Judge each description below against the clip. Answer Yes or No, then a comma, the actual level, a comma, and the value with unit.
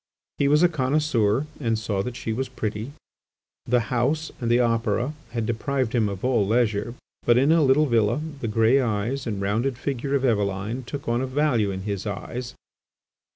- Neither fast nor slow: Yes, average, 185 wpm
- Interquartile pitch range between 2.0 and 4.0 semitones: Yes, average, 3.7 semitones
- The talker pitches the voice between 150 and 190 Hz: No, low, 120 Hz